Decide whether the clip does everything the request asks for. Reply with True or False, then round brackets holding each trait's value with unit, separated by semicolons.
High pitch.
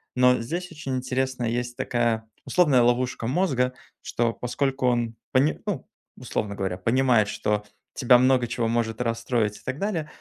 False (125 Hz)